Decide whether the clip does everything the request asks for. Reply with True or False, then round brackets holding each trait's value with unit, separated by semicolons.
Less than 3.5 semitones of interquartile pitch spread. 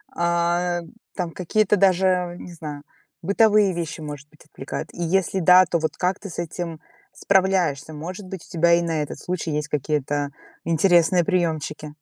True (3.0 semitones)